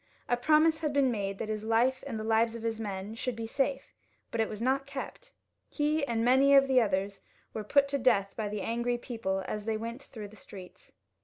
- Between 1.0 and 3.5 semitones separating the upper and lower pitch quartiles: No, average, 4.0 semitones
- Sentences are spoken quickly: Yes, fast, 225 wpm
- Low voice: No, high, 230 Hz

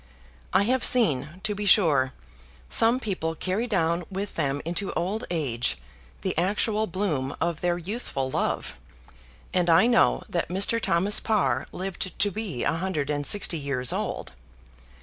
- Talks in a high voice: No, medium, 180 Hz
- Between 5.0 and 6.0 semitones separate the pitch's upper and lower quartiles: Yes, average, 5.3 semitones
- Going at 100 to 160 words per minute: Yes, average, 150 wpm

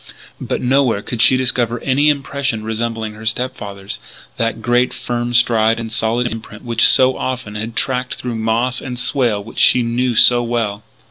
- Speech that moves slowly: No, average, 185 wpm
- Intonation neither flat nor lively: No, narrow, 2.1 semitones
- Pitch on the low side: Yes, low, 120 Hz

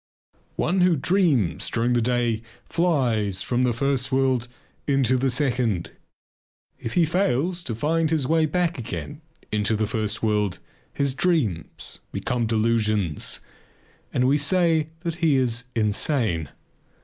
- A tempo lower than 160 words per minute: Yes, slow, 135 wpm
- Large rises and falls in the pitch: Yes, wide, 5.9 semitones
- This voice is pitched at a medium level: No, low, 125 Hz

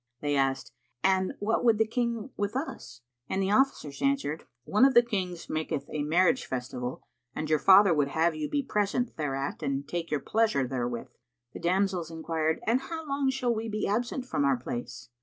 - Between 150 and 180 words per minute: No, average, 190 wpm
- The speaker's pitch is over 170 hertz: Yes, medium, 185 Hz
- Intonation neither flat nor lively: No, wide, 7.9 semitones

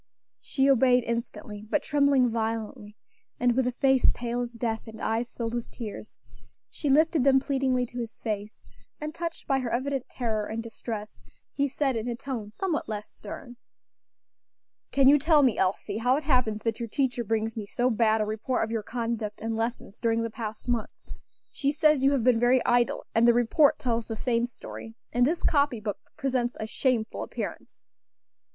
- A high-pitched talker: Yes, high, 240 Hz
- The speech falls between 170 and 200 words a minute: Yes, average, 185 wpm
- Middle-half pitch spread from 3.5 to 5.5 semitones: No, average, 3.1 semitones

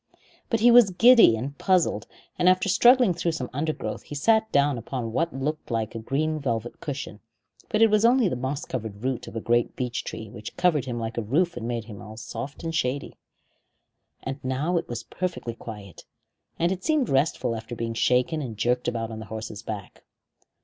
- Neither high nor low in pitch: No, low, 130 Hz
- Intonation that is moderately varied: No, wide, 7.1 semitones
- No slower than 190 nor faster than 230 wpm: Yes, average, 200 wpm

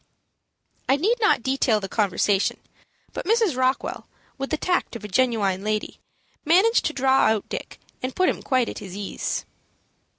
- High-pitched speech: Yes, very high, 255 Hz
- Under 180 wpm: Yes, average, 165 wpm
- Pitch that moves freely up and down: Yes, wide, 6.7 semitones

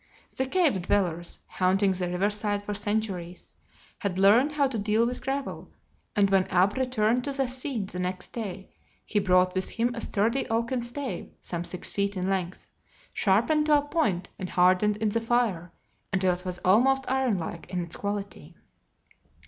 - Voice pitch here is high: Yes, high, 205 Hz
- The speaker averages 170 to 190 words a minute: Yes, average, 175 wpm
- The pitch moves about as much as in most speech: Yes, average, 4.7 semitones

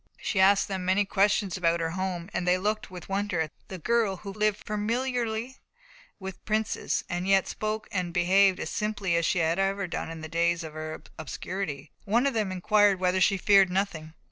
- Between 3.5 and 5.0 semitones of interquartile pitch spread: No, average, 3.0 semitones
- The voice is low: No, high, 190 Hz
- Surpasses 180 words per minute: Yes, average, 195 wpm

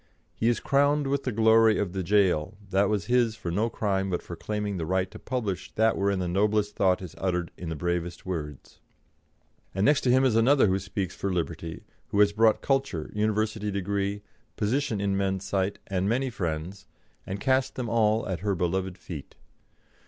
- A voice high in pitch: No, low, 100 Hz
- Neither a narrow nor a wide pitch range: Yes, average, 3.3 semitones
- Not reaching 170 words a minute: No, average, 190 wpm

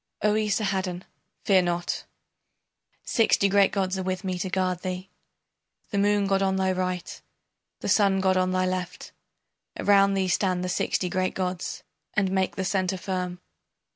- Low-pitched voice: No, high, 190 Hz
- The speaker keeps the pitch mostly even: Yes, narrow, 1.2 semitones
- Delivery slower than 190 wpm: Yes, average, 160 wpm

